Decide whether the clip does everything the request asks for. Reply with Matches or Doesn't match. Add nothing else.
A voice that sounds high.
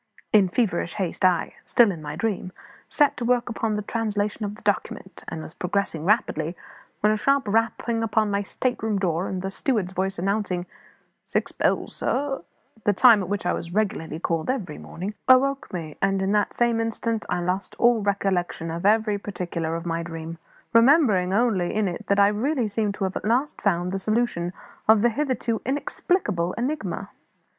Matches